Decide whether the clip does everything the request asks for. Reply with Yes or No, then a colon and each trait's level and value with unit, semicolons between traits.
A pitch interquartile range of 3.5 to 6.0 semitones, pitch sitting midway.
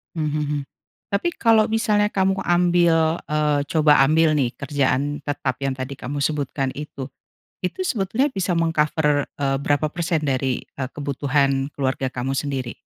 Yes: average, 4.0 semitones; medium, 150 Hz